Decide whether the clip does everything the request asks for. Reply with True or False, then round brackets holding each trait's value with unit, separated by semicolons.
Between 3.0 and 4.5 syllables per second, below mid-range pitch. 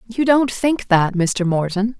False (3.9 syllables/s; 210 Hz)